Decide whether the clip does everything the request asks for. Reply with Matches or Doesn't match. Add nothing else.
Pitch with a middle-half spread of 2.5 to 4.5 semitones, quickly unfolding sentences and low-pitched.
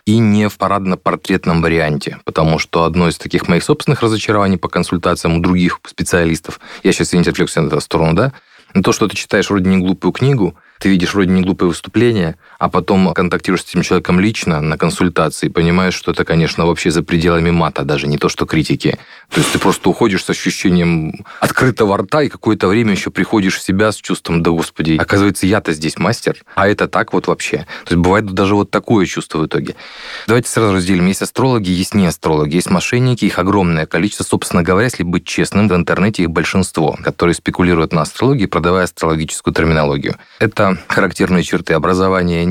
Matches